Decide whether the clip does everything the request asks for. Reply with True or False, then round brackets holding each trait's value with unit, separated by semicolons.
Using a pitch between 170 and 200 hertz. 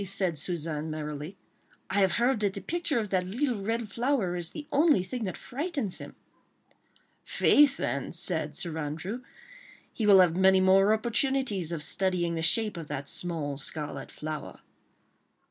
True (190 Hz)